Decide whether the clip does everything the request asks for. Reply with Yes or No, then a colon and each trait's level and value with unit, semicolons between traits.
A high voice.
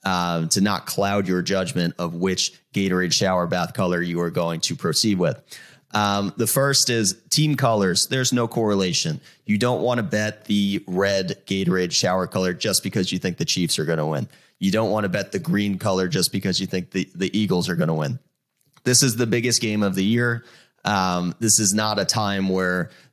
No: low, 100 Hz